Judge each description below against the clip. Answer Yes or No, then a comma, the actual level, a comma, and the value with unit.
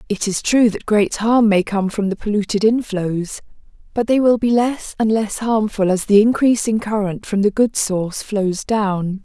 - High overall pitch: Yes, high, 210 Hz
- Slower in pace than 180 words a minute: No, average, 195 wpm